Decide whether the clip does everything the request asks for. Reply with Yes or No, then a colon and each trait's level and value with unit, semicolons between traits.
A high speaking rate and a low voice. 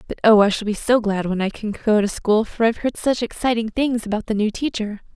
No: fast, 270 wpm; high, 220 Hz